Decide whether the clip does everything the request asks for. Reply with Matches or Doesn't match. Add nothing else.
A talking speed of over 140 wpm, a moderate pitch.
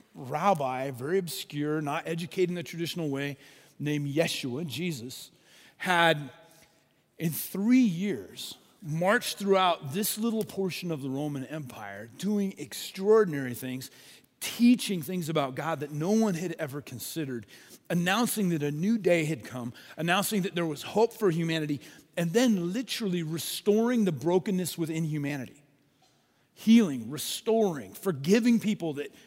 Doesn't match